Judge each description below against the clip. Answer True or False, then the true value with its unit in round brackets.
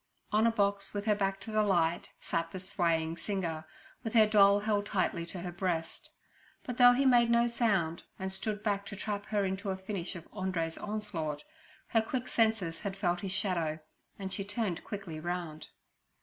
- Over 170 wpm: True (190 wpm)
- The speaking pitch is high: True (195 Hz)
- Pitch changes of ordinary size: True (3.4 semitones)